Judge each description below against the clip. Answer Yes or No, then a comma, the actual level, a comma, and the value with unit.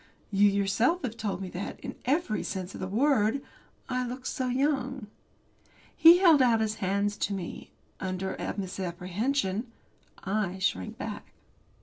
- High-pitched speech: Yes, high, 210 Hz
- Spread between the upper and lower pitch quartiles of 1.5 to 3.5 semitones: No, average, 5.1 semitones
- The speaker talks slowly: No, average, 145 wpm